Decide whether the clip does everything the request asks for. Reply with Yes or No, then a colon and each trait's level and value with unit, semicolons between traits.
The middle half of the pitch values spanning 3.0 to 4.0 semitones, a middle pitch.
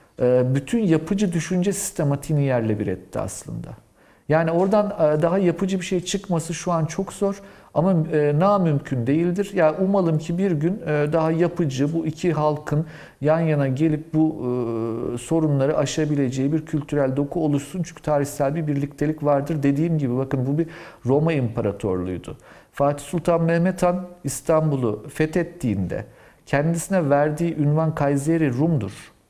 Yes: average, 3.3 semitones; medium, 155 Hz